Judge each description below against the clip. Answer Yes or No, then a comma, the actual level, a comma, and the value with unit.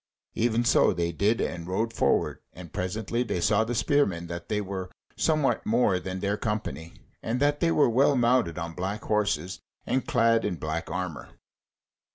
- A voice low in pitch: Yes, low, 105 Hz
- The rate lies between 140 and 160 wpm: No, average, 175 wpm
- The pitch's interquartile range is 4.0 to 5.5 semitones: Yes, average, 4.9 semitones